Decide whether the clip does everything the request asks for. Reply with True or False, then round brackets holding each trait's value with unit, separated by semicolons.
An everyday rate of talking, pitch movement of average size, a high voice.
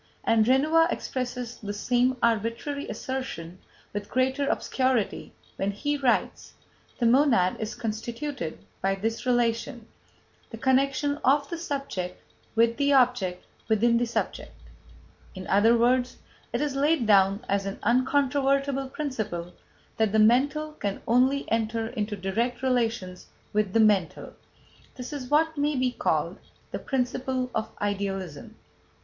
False (130 wpm; 4.0 semitones; 240 Hz)